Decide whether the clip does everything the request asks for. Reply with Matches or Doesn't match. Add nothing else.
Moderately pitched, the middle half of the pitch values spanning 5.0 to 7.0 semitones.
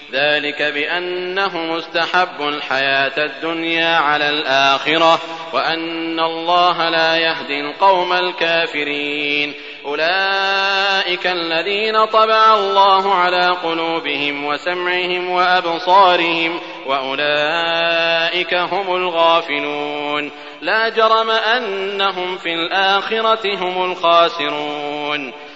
Doesn't match